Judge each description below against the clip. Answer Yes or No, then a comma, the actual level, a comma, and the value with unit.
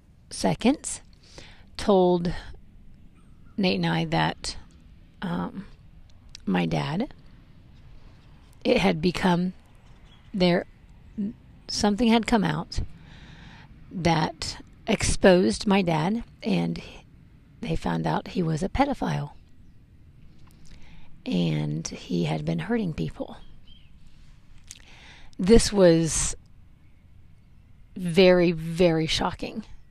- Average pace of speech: No, slow, 80 wpm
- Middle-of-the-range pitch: Yes, medium, 165 Hz